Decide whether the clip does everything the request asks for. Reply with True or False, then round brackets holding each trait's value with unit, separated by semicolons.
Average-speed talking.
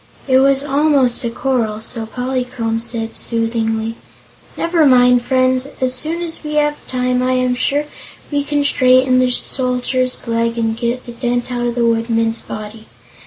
True (165 wpm)